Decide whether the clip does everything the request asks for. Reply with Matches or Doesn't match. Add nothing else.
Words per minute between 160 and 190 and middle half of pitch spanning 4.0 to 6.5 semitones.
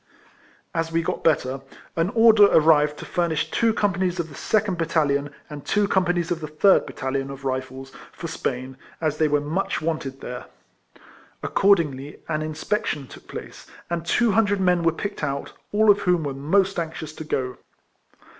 Matches